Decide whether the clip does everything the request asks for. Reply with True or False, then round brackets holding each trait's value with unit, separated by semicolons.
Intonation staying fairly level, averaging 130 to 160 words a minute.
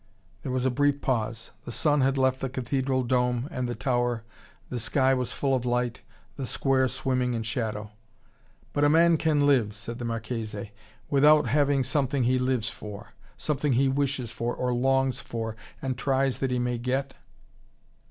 False (2.1 semitones; 175 wpm)